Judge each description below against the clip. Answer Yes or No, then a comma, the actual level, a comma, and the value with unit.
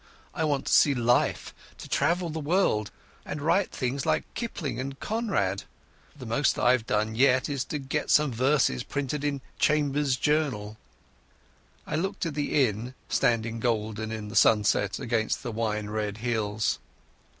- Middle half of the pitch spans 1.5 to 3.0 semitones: No, average, 5.1 semitones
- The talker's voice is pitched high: No, low, 125 Hz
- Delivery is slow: No, average, 155 wpm